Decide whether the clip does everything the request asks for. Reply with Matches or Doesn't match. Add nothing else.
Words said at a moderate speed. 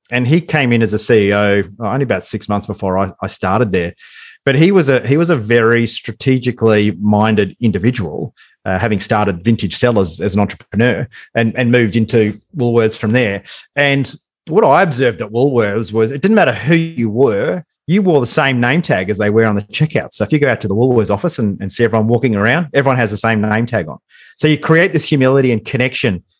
Doesn't match